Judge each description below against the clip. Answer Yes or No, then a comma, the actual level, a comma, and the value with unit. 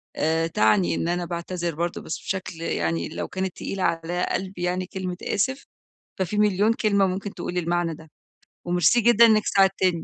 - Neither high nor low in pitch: Yes, medium, 180 Hz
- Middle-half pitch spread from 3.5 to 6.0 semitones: No, average, 2.7 semitones